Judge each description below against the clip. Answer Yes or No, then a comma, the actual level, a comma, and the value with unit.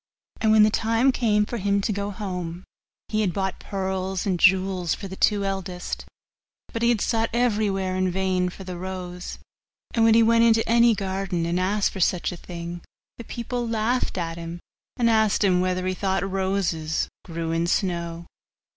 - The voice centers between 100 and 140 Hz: No, high, 190 Hz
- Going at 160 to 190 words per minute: Yes, average, 185 wpm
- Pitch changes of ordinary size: Yes, average, 3.2 semitones